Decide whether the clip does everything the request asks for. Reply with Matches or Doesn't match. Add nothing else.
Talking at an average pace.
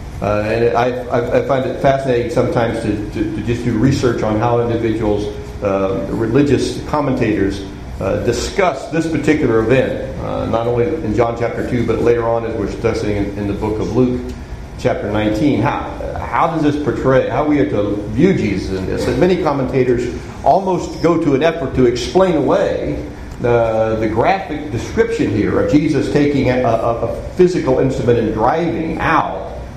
Matches